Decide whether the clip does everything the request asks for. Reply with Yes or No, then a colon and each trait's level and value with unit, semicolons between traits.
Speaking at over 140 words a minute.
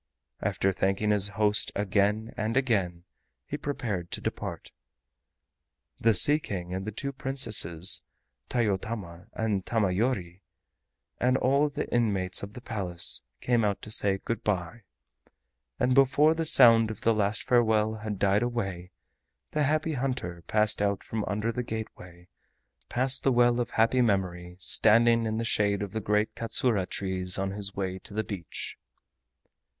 Yes: average, 155 wpm